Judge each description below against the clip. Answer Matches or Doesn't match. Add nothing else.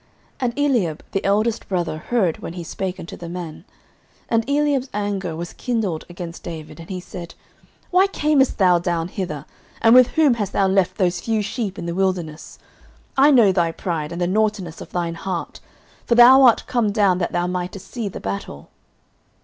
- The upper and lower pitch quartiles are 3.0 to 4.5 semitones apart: Doesn't match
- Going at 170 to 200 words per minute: Matches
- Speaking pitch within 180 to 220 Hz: Matches